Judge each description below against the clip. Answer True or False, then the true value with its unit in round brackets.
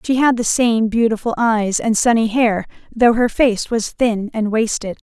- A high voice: True (225 Hz)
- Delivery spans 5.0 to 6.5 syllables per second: False (4.3 syllables/s)